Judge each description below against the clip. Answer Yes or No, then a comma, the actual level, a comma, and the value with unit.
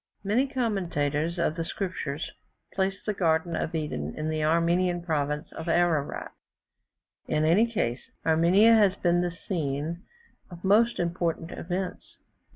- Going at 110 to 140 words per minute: Yes, slow, 135 wpm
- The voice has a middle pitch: Yes, medium, 170 Hz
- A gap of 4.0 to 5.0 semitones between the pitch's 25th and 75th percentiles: No, average, 3.3 semitones